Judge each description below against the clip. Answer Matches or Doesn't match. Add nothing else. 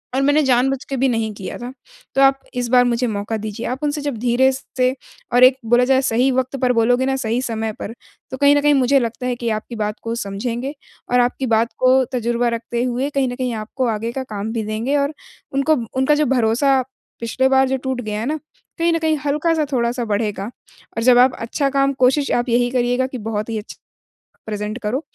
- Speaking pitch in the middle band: Doesn't match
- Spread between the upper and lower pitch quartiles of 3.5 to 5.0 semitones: Doesn't match